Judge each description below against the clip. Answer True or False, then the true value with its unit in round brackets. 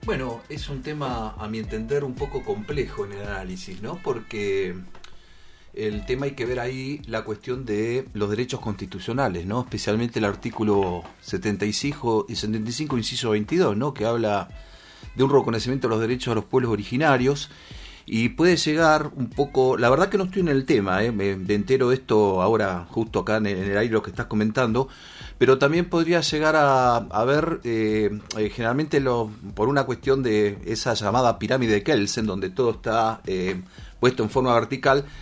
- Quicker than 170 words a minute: True (180 wpm)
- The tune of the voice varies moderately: True (4.1 semitones)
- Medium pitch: False (115 Hz)